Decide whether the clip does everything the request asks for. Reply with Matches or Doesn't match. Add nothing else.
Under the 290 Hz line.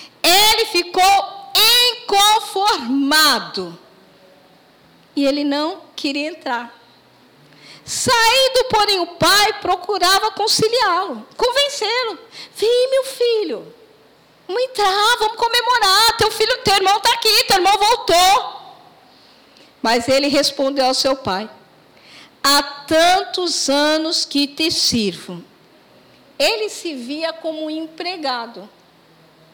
Doesn't match